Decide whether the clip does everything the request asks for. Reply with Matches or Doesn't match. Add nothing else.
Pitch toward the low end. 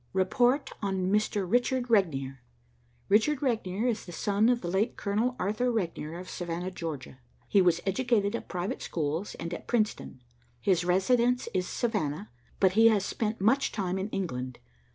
Doesn't match